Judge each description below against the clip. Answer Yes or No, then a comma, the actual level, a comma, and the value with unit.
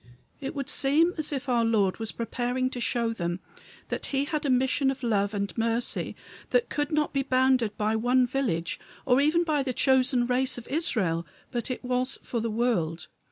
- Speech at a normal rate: Yes, average, 190 wpm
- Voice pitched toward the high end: Yes, very high, 250 Hz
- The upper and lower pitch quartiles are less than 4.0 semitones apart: Yes, average, 3.2 semitones